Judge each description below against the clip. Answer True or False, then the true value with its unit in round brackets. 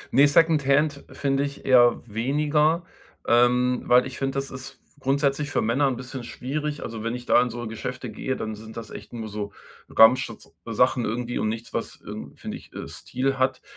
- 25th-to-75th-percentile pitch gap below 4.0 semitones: True (2.8 semitones)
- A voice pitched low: True (125 Hz)